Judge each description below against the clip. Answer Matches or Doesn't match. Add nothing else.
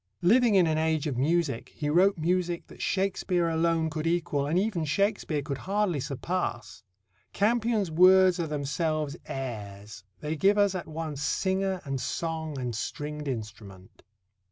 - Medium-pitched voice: Matches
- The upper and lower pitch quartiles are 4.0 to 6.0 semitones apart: Matches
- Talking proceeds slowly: Doesn't match